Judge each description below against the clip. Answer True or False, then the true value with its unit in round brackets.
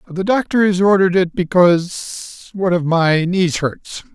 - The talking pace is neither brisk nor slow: True (160 wpm)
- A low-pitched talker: False (180 Hz)